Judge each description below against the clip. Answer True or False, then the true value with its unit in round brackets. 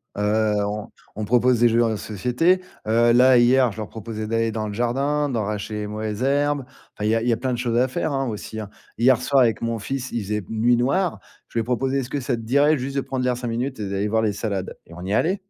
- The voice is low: True (120 Hz)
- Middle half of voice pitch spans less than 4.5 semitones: True (3.2 semitones)